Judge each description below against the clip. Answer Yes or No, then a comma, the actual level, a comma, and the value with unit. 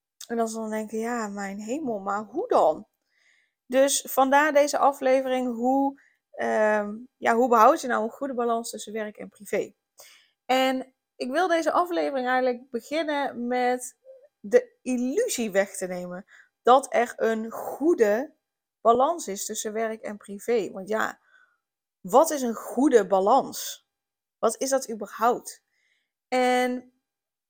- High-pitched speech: Yes, very high, 250 Hz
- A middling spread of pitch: Yes, average, 3.8 semitones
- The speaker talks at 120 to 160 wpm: Yes, average, 140 wpm